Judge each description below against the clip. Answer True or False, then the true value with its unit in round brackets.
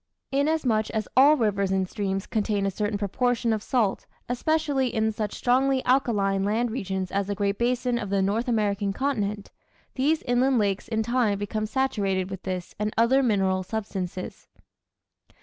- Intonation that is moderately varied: True (3.9 semitones)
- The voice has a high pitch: True (215 Hz)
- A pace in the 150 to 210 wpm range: True (160 wpm)